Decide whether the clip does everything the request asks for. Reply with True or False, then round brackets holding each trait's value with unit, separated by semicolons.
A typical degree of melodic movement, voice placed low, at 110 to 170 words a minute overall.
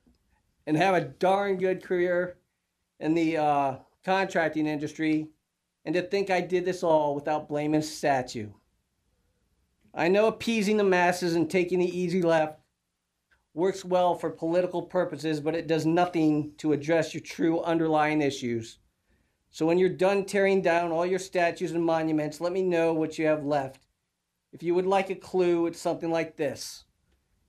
False (3.0 semitones; 165 Hz; 165 wpm)